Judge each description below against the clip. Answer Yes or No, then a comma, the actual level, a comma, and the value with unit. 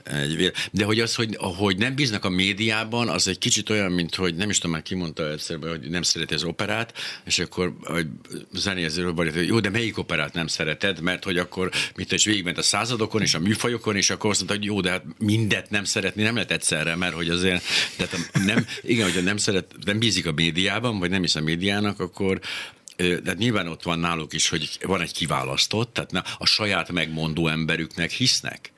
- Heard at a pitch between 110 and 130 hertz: No, very low, 95 Hz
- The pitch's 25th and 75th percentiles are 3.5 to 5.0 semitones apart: Yes, average, 3.8 semitones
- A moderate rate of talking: No, fast, 200 wpm